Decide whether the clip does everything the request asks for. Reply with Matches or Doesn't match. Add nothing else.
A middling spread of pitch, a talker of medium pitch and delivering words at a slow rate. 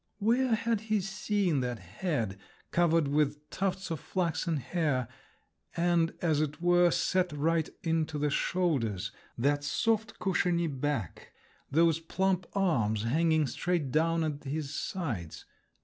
Matches